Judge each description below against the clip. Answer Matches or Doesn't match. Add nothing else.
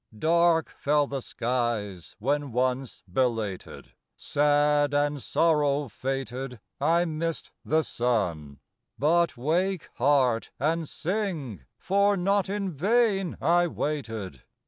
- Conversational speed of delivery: Doesn't match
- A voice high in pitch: Doesn't match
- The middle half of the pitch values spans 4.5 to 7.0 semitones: Matches